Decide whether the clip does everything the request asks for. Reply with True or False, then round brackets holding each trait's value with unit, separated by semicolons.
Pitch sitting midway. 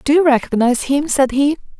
False (275 Hz)